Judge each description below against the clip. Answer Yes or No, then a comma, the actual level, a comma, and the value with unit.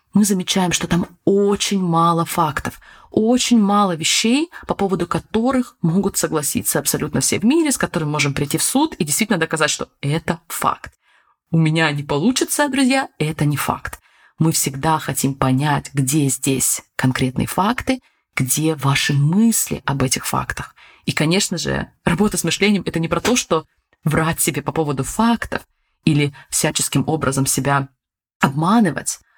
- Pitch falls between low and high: Yes, medium, 165 Hz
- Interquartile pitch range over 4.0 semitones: Yes, wide, 5.6 semitones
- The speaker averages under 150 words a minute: No, average, 155 wpm